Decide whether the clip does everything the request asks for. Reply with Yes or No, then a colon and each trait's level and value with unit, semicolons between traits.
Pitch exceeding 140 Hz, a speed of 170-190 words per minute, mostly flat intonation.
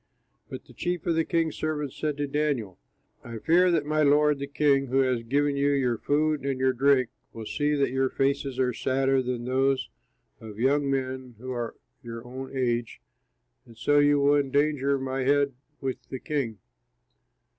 No: low, 135 Hz; average, 180 wpm; narrow, 2.3 semitones